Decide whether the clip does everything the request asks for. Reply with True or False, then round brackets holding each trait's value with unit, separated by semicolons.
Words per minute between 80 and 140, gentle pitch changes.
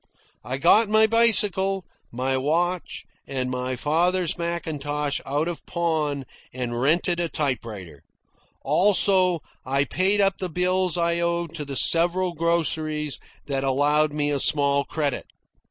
False (135 wpm; 4.1 semitones)